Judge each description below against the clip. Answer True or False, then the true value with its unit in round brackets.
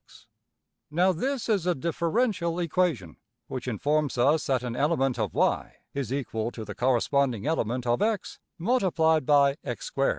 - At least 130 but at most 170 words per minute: True (135 wpm)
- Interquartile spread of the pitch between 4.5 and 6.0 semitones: True (5.5 semitones)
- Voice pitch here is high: False (145 Hz)